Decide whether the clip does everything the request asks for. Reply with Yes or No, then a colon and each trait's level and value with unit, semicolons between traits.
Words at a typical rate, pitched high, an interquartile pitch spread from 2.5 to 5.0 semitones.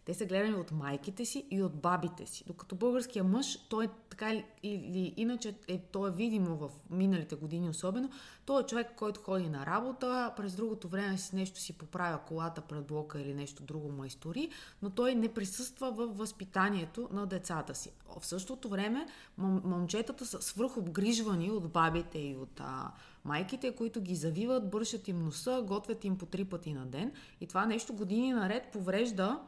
No: fast, 180 wpm; high, 195 Hz; average, 4.6 semitones